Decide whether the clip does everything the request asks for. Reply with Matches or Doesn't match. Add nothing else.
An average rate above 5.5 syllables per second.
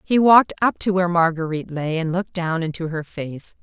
Matches